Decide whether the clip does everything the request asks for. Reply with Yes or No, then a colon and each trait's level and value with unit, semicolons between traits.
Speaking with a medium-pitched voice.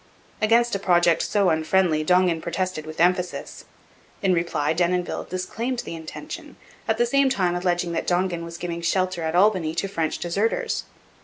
Yes: medium, 180 Hz